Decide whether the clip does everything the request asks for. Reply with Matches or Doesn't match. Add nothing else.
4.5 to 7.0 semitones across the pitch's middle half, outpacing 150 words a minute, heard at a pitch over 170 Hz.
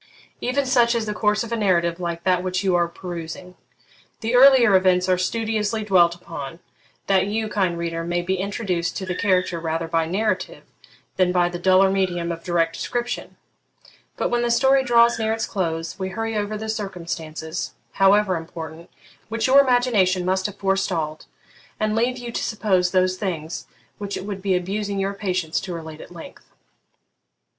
Doesn't match